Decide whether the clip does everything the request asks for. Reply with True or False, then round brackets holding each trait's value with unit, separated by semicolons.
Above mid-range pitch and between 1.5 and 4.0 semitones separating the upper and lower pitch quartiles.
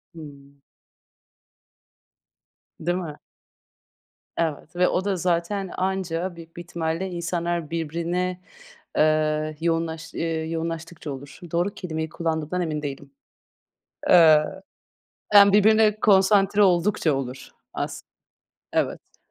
False (170 Hz; 2.6 semitones)